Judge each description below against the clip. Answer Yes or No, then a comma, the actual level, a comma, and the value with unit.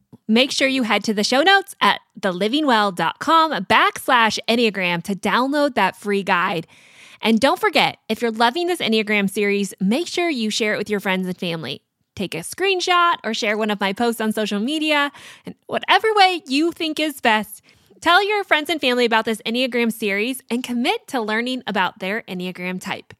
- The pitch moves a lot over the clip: Yes, wide, 6.2 semitones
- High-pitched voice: Yes, high, 230 Hz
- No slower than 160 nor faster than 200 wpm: Yes, average, 185 wpm